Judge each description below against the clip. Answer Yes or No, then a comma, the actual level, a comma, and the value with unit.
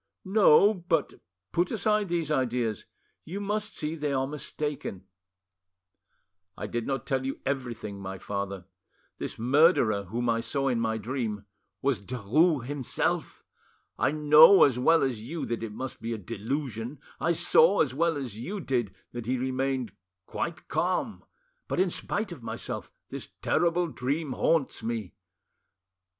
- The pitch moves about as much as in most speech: No, wide, 6.0 semitones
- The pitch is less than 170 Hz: Yes, low, 135 Hz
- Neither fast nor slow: Yes, average, 145 wpm